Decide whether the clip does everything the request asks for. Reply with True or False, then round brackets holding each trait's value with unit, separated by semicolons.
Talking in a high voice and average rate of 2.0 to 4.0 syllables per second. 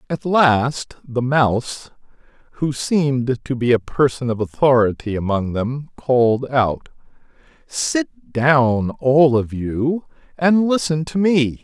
False (135 Hz; 3.6 syllables/s)